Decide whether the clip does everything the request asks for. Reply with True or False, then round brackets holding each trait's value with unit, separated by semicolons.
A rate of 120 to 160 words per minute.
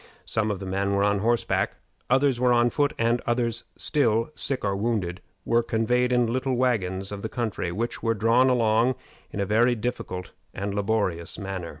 False (185 wpm)